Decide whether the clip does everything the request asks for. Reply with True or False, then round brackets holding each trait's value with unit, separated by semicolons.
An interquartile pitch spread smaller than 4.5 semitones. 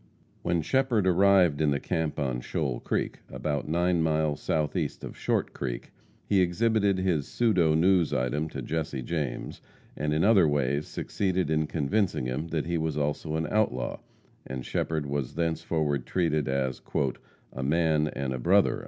True (3.6 semitones)